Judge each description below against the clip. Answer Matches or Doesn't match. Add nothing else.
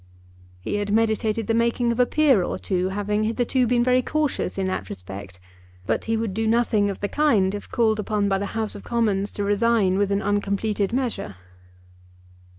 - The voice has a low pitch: Doesn't match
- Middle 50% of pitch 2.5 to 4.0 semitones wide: Matches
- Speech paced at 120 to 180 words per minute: Doesn't match